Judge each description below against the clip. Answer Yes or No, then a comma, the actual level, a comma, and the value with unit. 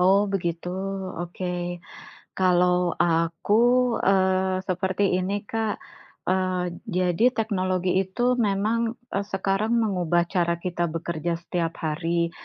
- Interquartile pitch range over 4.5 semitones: No, narrow, 2.6 semitones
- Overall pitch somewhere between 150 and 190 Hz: Yes, medium, 185 Hz